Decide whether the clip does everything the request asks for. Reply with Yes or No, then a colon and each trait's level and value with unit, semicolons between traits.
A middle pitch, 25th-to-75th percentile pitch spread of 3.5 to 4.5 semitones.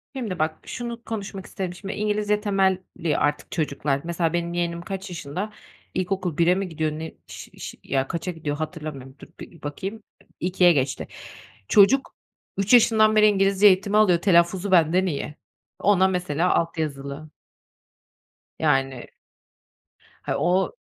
Yes: medium, 180 Hz; average, 3.9 semitones